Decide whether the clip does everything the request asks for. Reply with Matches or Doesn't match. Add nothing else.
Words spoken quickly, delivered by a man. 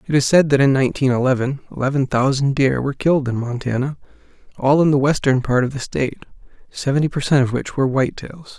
Matches